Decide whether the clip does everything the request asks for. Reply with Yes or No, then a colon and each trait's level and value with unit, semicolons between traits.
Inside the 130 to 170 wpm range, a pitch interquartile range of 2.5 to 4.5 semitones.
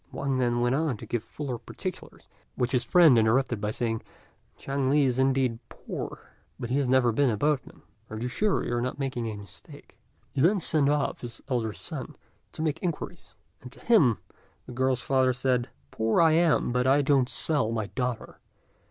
No: average, 195 wpm; average, 2.9 semitones